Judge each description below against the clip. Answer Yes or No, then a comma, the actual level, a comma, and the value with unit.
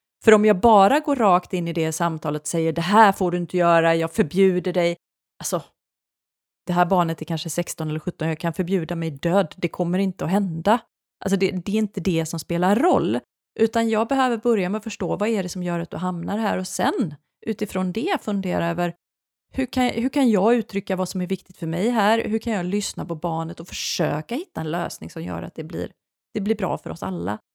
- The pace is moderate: No, fast, 230 wpm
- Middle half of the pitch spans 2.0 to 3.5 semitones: No, average, 4.0 semitones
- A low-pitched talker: No, medium, 185 Hz